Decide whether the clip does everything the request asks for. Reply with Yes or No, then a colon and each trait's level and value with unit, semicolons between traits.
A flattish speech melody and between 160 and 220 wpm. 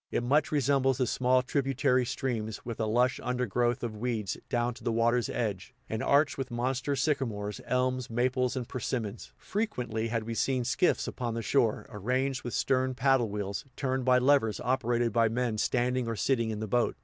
Yes: narrow, 2.2 semitones; average, 185 wpm